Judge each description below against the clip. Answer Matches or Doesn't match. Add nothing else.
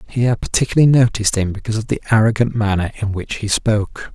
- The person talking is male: Matches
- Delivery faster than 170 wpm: Matches